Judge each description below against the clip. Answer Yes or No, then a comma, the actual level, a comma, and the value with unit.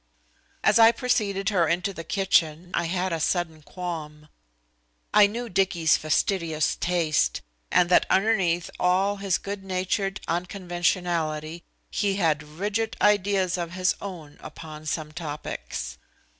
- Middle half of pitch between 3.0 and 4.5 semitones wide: Yes, average, 3.4 semitones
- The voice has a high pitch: No, medium, 180 Hz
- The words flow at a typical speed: No, slow, 130 wpm